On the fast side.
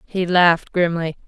No: average, 140 wpm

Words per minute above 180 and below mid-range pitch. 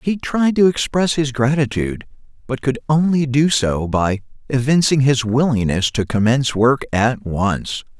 No: average, 150 wpm; low, 130 Hz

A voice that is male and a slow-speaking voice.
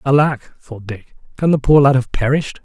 No: male; fast, 205 wpm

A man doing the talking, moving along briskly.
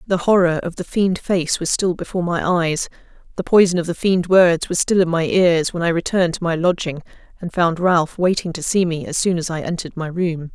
No: female; fast, 240 wpm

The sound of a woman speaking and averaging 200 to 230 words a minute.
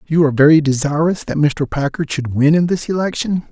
No: male; fast, 205 wpm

